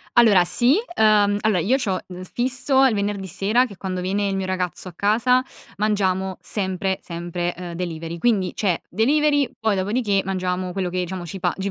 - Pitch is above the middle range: Yes, high, 195 Hz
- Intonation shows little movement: No, average, 3.1 semitones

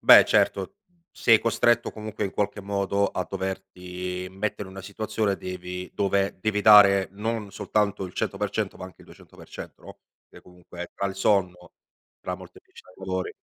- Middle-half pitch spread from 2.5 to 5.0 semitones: No, narrow, 2.0 semitones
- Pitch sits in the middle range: No, low, 100 Hz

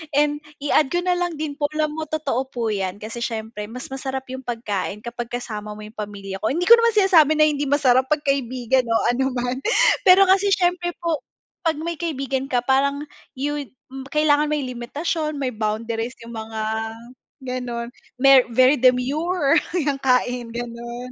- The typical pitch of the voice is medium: No, very high, 265 Hz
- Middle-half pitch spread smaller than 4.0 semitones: No, average, 4.3 semitones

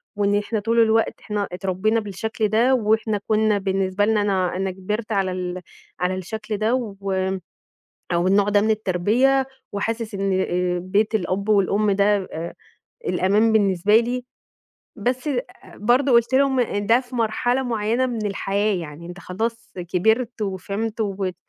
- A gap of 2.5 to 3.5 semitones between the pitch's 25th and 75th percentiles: Yes, average, 2.8 semitones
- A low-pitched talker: No, high, 210 Hz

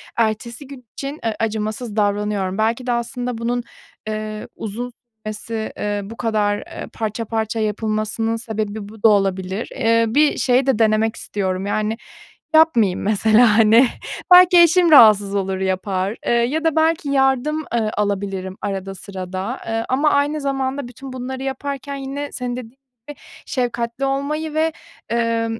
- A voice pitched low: No, high, 225 Hz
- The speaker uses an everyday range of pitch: Yes, average, 4.1 semitones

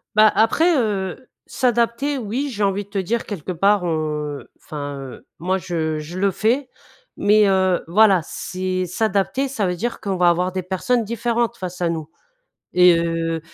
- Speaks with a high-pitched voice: Yes, high, 195 Hz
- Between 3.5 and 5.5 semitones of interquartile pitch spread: Yes, average, 4.2 semitones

